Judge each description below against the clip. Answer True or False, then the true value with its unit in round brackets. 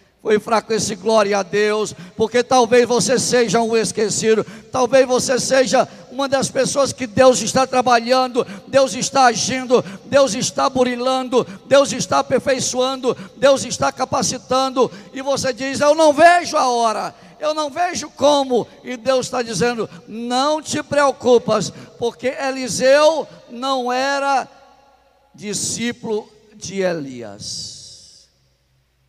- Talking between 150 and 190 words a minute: False (125 wpm)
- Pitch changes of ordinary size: True (3.5 semitones)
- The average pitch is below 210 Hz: False (250 Hz)